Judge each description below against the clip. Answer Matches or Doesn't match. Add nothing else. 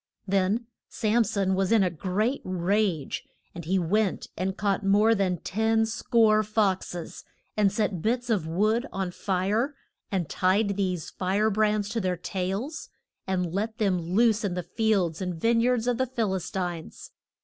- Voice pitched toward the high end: Matches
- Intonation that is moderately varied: Matches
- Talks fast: Doesn't match